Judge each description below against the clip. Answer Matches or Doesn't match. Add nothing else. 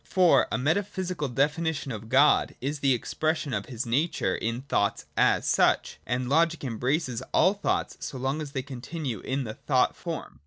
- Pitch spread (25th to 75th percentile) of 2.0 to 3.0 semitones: Doesn't match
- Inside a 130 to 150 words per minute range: Doesn't match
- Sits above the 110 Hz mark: Matches